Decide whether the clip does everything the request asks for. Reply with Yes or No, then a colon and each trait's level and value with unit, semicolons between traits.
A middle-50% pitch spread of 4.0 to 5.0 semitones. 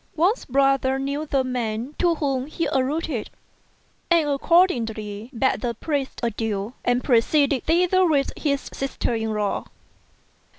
Yes: average, 4.6 semitones